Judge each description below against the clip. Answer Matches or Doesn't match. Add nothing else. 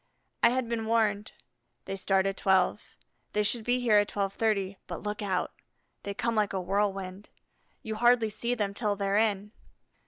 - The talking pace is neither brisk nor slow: Matches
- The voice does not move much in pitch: Matches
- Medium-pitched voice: Doesn't match